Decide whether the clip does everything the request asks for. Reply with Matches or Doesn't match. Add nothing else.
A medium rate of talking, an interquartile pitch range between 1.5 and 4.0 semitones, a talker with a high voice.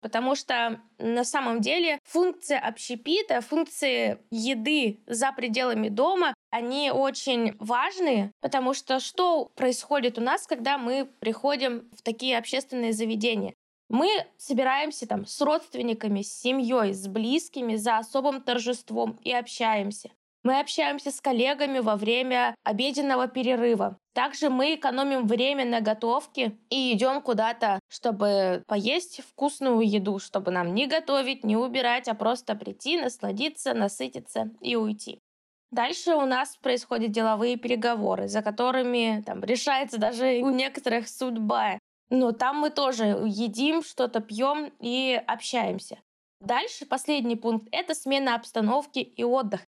Matches